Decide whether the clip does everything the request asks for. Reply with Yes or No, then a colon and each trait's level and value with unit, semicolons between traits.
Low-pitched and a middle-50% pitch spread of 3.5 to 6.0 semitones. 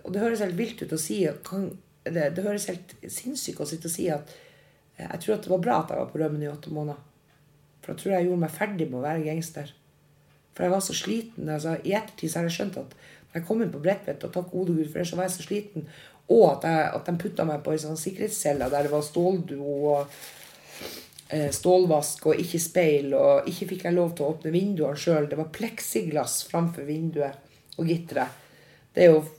No: medium, 165 Hz; average, 3.9 semitones